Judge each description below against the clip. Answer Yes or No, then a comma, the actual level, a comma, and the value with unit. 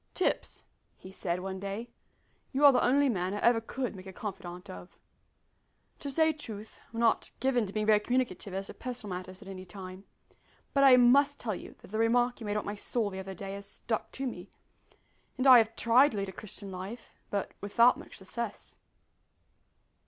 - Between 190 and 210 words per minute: Yes, average, 200 wpm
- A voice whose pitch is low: No, high, 215 Hz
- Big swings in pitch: No, average, 4.2 semitones